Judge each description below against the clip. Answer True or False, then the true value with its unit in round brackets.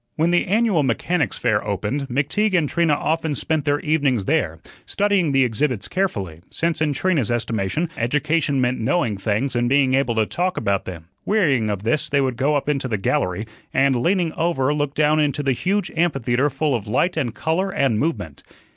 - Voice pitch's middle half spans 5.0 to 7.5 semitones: True (5.4 semitones)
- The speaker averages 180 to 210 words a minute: True (190 wpm)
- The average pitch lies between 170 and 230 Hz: False (140 Hz)